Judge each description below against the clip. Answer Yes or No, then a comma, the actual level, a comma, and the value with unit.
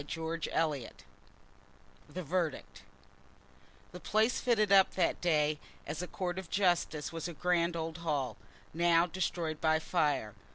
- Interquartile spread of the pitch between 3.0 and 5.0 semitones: No, narrow, 2.4 semitones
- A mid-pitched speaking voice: Yes, medium, 170 Hz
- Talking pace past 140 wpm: No, slow, 135 wpm